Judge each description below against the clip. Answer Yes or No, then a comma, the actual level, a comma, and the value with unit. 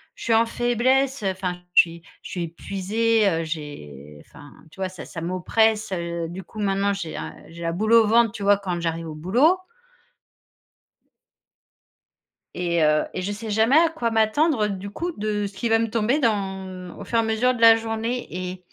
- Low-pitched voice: No, high, 200 Hz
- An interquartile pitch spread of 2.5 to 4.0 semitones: No, average, 4.5 semitones